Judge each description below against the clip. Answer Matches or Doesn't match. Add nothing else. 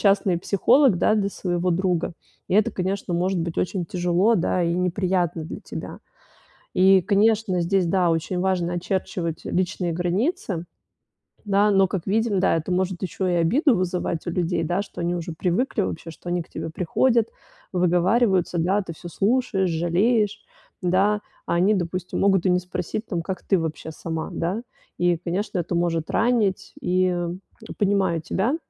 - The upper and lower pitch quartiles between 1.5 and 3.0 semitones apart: Matches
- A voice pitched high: Doesn't match